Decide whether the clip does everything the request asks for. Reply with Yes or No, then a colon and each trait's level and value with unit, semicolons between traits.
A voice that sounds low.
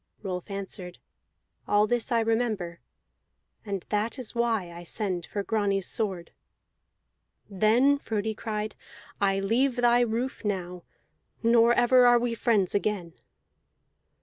No: high, 215 Hz